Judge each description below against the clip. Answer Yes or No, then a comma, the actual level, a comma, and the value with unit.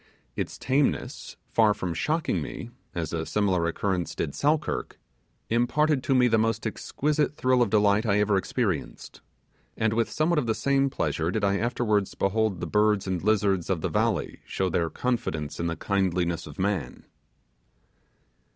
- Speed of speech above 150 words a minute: Yes, average, 160 wpm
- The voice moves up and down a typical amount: Yes, average, 4.8 semitones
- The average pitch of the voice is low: Yes, low, 105 Hz